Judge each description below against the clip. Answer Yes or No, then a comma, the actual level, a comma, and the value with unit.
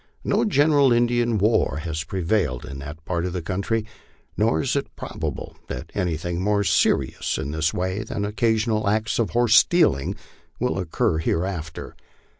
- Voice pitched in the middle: No, low, 100 Hz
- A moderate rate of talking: Yes, average, 160 wpm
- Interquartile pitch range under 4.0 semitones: No, average, 5.3 semitones